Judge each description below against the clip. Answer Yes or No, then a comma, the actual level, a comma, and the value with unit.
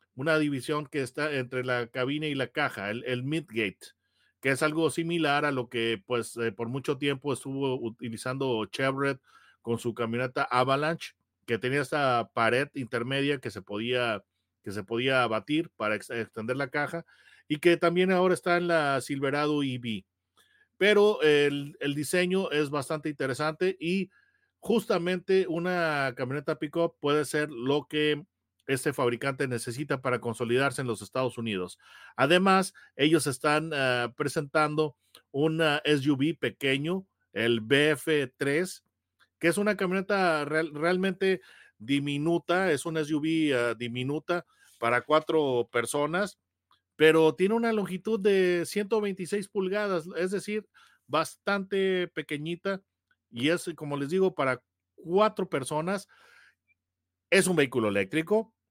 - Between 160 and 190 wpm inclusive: No, average, 135 wpm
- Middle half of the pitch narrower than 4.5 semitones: No, wide, 5.4 semitones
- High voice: No, medium, 150 Hz